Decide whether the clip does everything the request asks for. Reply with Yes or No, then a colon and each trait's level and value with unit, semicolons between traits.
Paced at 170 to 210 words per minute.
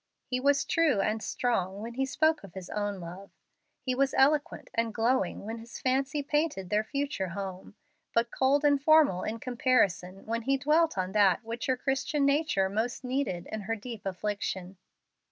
Yes: average, 175 wpm